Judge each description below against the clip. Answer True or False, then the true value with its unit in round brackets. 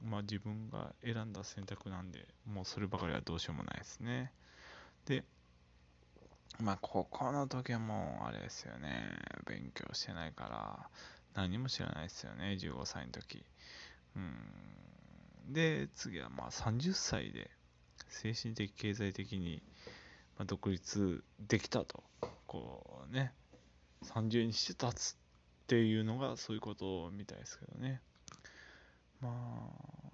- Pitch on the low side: True (100 Hz)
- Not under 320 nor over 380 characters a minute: False (235 characters per minute)